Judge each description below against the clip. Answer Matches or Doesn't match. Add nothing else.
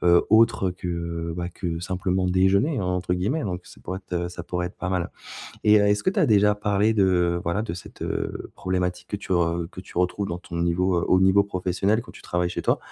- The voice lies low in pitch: Matches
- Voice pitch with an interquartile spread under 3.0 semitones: Matches